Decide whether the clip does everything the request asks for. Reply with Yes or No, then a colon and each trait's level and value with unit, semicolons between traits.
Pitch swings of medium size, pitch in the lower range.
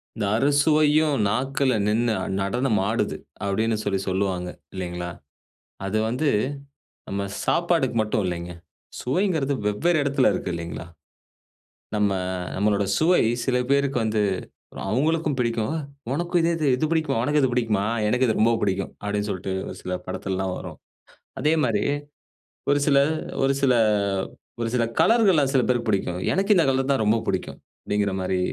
No: wide, 6.2 semitones; low, 120 Hz